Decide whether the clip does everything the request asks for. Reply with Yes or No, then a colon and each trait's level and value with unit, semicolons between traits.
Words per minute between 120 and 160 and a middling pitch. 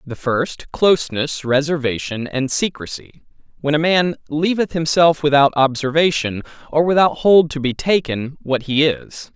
Yes: average, 140 wpm; medium, 145 Hz